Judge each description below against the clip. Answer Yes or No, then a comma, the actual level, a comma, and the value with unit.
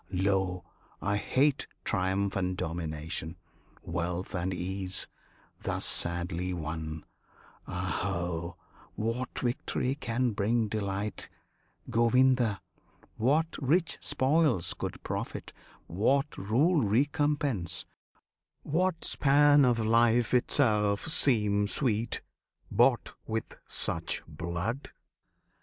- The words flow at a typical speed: No, slow, 90 wpm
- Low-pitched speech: Yes, low, 105 Hz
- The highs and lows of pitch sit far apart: Yes, wide, 6.2 semitones